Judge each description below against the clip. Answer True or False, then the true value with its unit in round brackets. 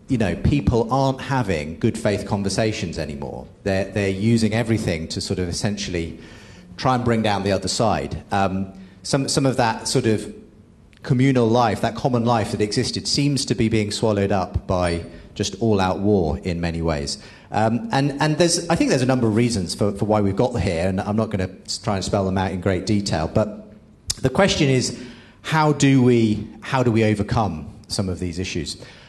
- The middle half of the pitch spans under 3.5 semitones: False (4.1 semitones)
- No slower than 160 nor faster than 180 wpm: False (200 wpm)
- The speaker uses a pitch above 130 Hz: False (105 Hz)